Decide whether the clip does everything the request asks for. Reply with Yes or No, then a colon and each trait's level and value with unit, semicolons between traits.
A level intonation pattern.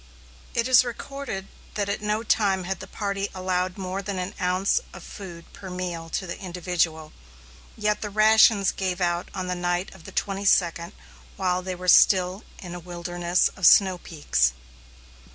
Yes: narrow, 2.1 semitones